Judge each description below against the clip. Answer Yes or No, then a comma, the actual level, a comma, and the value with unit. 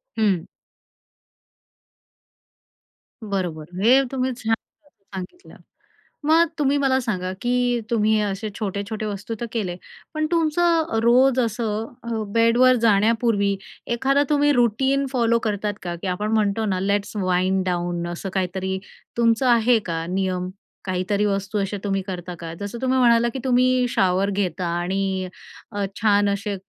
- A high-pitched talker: Yes, high, 210 Hz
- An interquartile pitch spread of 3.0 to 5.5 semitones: Yes, average, 4.1 semitones